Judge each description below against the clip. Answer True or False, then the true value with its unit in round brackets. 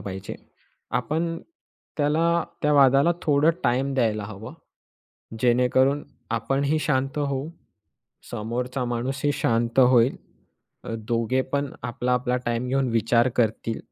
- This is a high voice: False (125 Hz)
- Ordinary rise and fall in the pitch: True (3.2 semitones)